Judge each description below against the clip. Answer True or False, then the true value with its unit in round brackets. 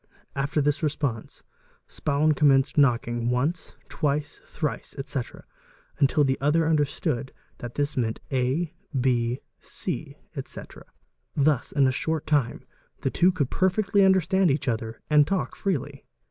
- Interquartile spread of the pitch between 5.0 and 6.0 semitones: False (3.4 semitones)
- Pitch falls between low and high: True (145 Hz)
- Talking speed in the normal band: False (130 wpm)